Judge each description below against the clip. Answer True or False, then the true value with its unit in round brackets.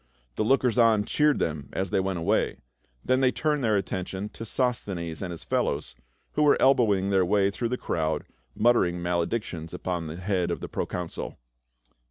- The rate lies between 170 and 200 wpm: True (180 wpm)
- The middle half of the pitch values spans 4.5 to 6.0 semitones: True (5.2 semitones)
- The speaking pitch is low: True (95 Hz)